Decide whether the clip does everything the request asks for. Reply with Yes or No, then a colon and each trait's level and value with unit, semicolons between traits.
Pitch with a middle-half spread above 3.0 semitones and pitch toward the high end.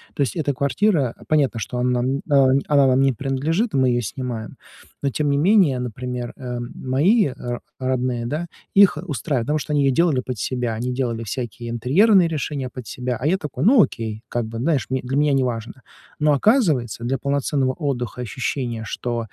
No: average, 3.4 semitones; low, 130 Hz